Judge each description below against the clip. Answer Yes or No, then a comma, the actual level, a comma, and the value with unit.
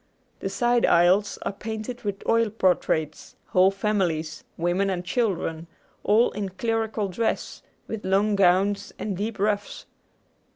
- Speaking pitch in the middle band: No, high, 200 Hz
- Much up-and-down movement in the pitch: No, average, 2.9 semitones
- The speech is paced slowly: Yes, slow, 130 wpm